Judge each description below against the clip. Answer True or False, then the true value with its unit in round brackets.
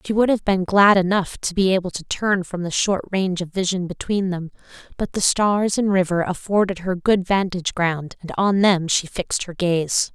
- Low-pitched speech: False (185 Hz)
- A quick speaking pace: True (215 wpm)